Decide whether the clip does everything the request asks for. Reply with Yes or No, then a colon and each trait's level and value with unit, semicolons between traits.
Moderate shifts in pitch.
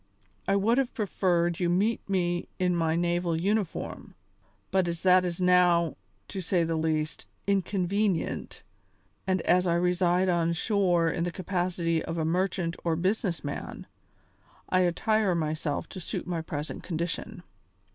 No: narrow, 2.0 semitones